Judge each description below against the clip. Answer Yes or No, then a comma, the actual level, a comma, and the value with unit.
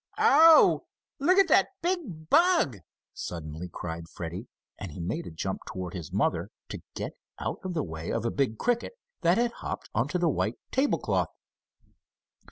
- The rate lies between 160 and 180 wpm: Yes, average, 170 wpm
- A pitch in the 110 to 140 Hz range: Yes, low, 135 Hz